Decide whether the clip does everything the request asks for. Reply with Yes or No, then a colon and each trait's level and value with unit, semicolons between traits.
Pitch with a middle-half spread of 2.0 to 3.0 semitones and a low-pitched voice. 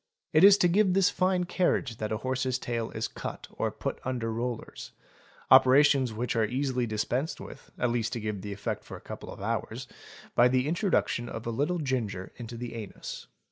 No: average, 4.1 semitones; low, 125 Hz